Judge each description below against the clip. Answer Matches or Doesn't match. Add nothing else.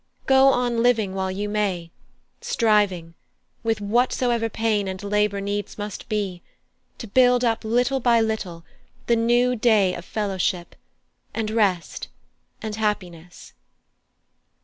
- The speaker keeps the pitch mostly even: Doesn't match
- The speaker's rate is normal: Doesn't match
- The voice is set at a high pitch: Matches